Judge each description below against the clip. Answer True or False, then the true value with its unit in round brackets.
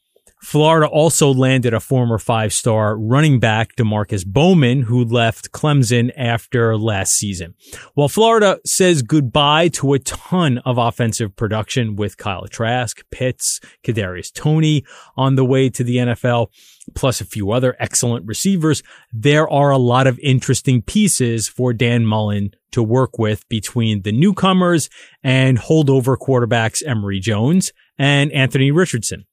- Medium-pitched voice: False (125 Hz)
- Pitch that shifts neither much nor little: True (4.0 semitones)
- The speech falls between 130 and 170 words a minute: True (140 wpm)